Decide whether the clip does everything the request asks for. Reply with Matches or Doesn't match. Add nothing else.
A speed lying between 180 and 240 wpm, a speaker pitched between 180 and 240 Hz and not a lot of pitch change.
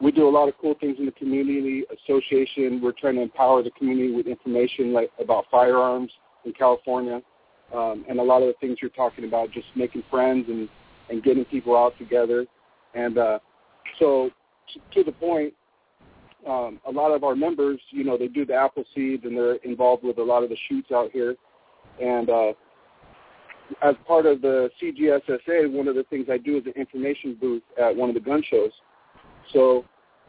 Doesn't match